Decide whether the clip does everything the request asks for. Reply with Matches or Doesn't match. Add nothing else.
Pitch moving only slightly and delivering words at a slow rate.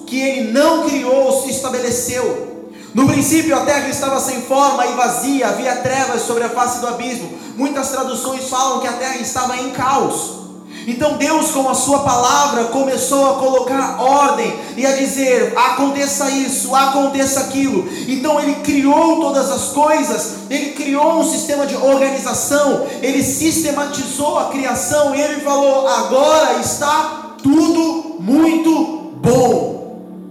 Doesn't match